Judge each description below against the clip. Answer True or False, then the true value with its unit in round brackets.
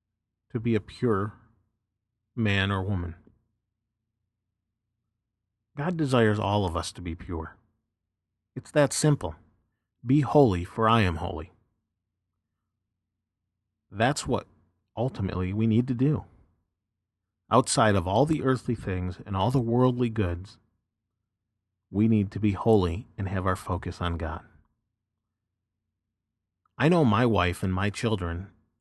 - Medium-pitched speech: False (105 Hz)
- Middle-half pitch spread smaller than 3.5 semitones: True (2.9 semitones)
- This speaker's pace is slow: True (125 wpm)